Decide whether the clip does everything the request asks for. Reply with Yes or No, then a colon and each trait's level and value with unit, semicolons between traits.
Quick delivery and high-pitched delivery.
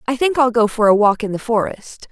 Yes: fast, 285 wpm; high, 230 Hz